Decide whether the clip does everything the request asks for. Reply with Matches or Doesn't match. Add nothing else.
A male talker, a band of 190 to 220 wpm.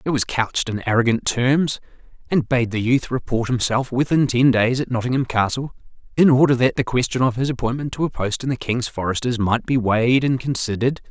Matches